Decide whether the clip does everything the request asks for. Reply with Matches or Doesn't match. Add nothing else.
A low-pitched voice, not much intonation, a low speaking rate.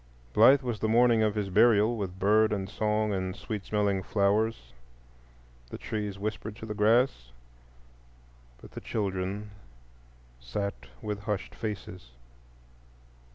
Matches